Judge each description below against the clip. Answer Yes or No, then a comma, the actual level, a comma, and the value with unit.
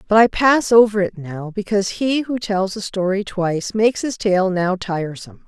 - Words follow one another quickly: No, average, 195 wpm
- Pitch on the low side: No, high, 200 Hz